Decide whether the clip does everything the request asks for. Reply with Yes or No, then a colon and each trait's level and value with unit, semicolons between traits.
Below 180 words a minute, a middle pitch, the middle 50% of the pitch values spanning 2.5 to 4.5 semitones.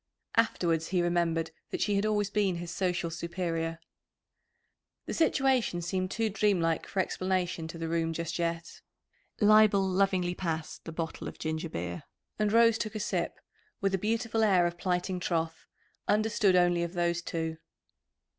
Yes: average, 155 wpm; medium, 180 Hz; average, 3.4 semitones